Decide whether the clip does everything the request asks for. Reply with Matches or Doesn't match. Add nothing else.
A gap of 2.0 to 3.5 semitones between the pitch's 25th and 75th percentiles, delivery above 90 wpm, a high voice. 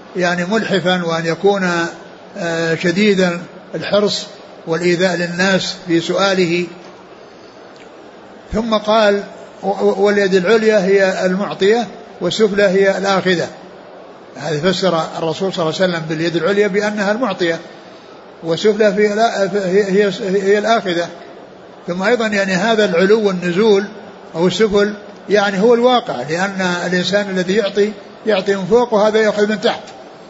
Matches